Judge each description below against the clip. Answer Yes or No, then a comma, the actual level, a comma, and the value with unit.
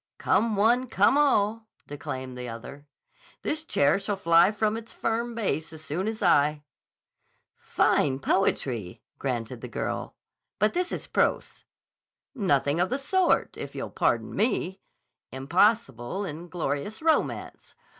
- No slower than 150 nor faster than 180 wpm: No, slow, 135 wpm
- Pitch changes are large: Yes, wide, 7.9 semitones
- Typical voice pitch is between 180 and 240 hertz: Yes, high, 190 Hz